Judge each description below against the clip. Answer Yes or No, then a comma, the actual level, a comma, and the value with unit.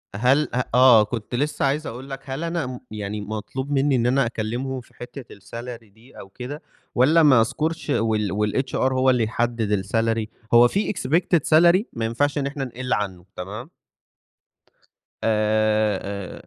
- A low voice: Yes, low, 120 Hz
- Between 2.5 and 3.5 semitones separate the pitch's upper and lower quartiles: No, average, 4.1 semitones